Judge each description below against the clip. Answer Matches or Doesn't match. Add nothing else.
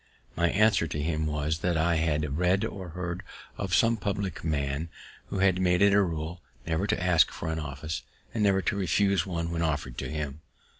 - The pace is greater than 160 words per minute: Matches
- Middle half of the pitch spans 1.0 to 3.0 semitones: Doesn't match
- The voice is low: Matches